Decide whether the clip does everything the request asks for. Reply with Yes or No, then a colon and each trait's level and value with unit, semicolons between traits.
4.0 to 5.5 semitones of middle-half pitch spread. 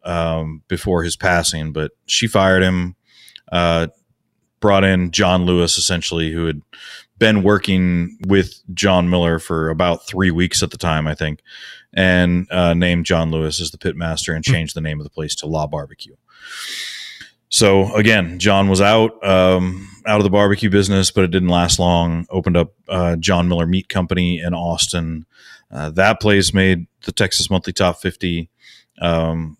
No: narrow, 2.4 semitones